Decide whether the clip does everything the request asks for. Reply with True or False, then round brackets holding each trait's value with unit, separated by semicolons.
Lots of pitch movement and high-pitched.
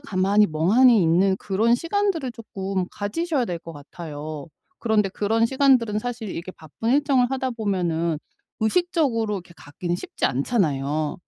True (6.3 semitones; 205 Hz)